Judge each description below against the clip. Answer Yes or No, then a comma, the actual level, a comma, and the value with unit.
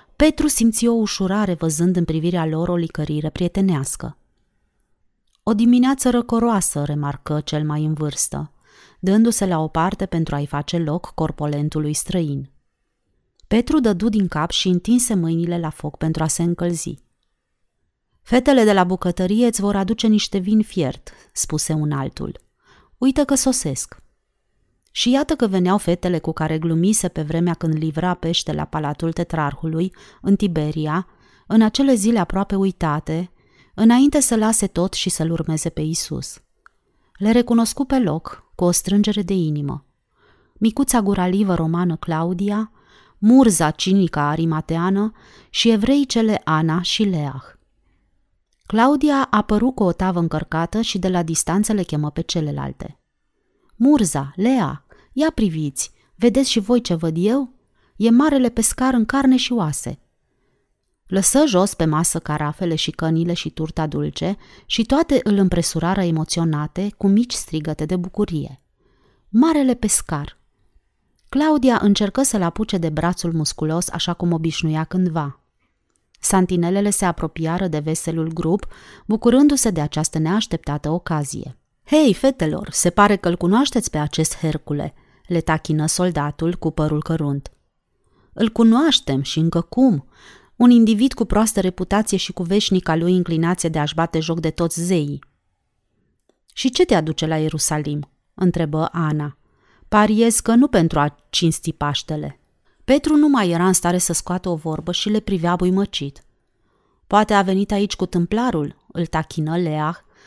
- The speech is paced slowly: No, average, 145 wpm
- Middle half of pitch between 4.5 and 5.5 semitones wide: Yes, average, 5.2 semitones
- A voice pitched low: No, medium, 175 Hz